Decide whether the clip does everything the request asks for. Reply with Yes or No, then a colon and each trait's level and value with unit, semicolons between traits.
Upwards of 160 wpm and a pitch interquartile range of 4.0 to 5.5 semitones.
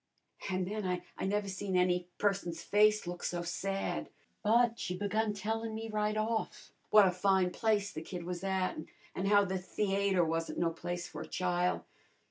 No: average, 175 wpm; average, 2.8 semitones